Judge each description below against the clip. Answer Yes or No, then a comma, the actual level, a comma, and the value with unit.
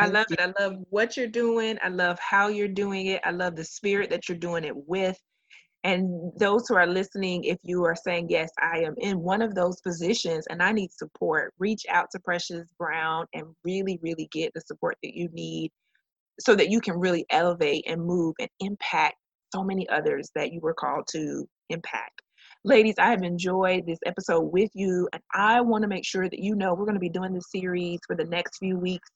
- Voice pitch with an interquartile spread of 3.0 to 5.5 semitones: No, narrow, 2.5 semitones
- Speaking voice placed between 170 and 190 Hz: Yes, medium, 185 Hz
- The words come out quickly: Yes, fast, 220 wpm